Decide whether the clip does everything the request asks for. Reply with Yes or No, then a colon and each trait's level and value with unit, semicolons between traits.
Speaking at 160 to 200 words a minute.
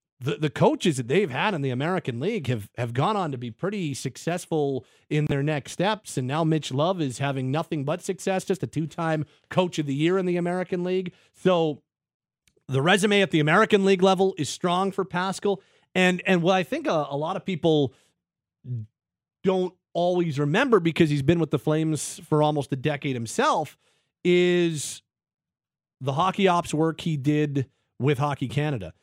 Yes: average, 180 wpm